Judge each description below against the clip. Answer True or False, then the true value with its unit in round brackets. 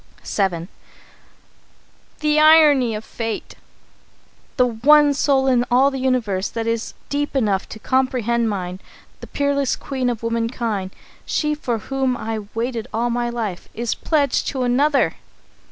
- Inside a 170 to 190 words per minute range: False (140 wpm)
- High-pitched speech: True (245 Hz)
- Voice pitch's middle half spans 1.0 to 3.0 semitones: False (3.4 semitones)